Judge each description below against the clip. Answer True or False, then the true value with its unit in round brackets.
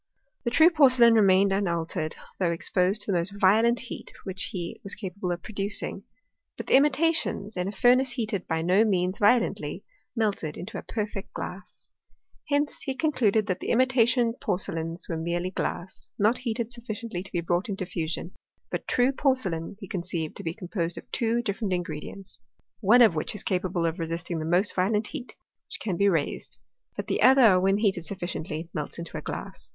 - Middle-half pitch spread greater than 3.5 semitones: True (4.7 semitones)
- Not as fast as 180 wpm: False (190 wpm)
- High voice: True (195 Hz)